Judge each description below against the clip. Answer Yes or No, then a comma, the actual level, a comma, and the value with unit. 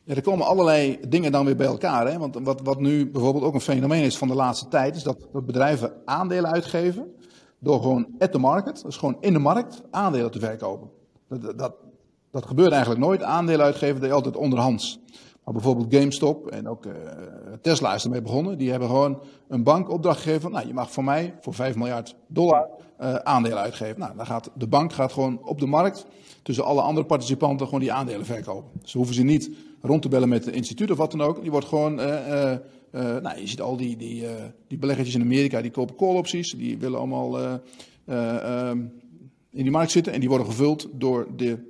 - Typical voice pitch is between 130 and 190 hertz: Yes, low, 135 Hz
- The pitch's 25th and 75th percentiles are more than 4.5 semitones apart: No, average, 3.7 semitones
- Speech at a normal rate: No, fast, 215 wpm